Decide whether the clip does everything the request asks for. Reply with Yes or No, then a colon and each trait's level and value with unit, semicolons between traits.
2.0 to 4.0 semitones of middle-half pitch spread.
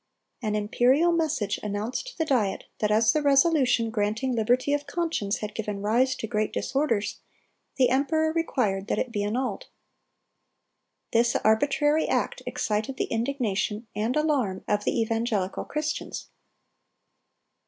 No: average, 5.1 semitones